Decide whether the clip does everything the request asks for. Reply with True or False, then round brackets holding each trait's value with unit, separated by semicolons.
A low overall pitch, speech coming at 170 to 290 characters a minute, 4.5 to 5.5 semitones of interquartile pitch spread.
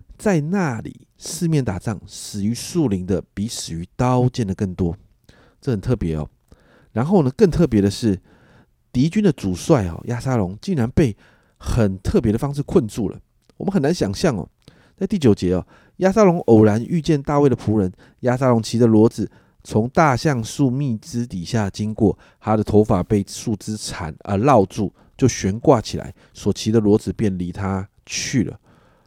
True (110 Hz; 250 characters per minute; 4.8 semitones)